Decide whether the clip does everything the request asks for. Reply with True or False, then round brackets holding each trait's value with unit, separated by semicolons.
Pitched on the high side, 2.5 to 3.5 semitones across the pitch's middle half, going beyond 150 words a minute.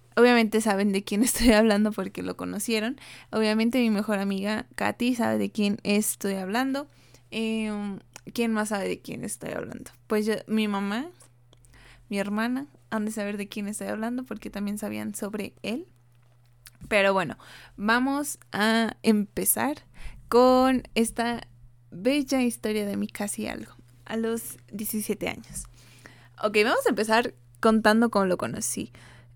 False (210 Hz; 3.1 semitones; 145 wpm)